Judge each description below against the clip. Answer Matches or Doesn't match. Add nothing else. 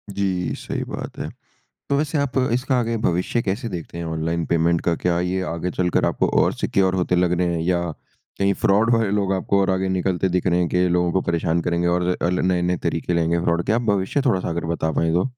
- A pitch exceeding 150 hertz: Doesn't match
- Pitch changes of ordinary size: Doesn't match